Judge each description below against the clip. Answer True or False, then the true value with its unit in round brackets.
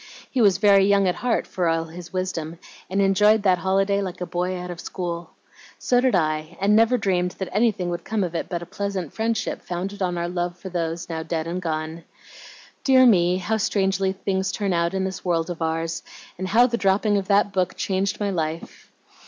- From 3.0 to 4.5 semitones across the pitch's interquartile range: False (2.6 semitones)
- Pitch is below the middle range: False (185 Hz)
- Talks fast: True (210 wpm)